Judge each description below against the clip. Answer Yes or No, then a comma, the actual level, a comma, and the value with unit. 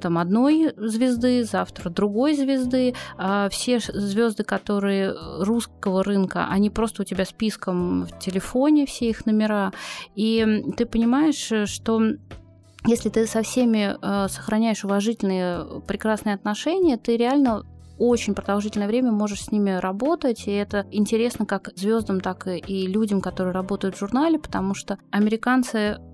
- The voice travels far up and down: No, average, 3.0 semitones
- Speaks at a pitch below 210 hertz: No, high, 215 Hz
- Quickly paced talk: No, average, 135 wpm